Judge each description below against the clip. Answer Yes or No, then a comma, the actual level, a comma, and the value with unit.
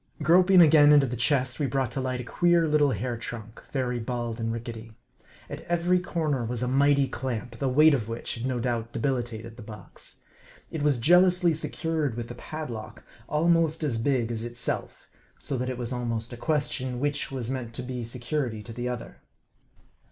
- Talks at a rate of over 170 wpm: Yes, average, 190 wpm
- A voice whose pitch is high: No, low, 125 Hz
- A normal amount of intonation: Yes, average, 4.0 semitones